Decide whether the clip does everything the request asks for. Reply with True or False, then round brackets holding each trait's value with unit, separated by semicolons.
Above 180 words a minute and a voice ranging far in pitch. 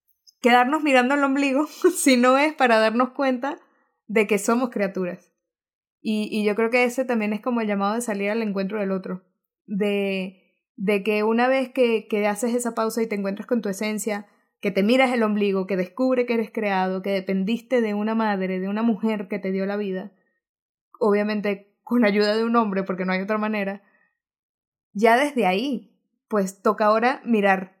False (190 wpm; 3.4 semitones)